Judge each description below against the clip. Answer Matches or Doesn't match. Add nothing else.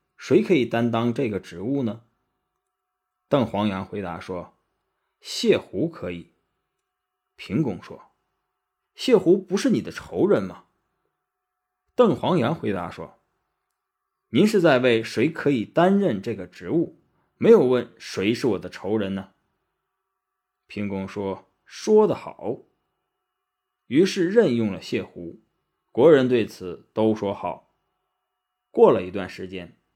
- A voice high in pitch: Doesn't match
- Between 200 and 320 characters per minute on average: Doesn't match